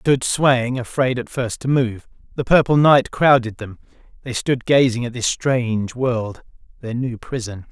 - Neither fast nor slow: Yes, average, 170 wpm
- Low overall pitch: Yes, low, 125 Hz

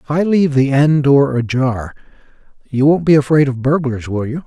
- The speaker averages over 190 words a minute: Yes, average, 200 wpm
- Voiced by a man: Yes, male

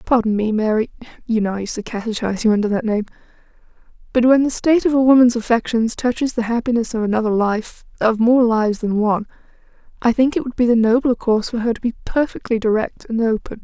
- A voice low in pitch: No, high, 230 Hz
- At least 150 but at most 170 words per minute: No, average, 195 wpm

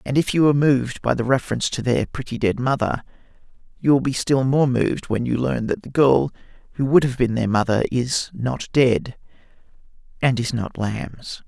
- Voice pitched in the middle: No, low, 130 Hz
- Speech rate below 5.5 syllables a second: Yes, 5.2 syllables/s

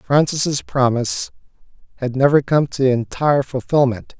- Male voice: Yes, male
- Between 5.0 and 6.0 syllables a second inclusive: No, 4.6 syllables/s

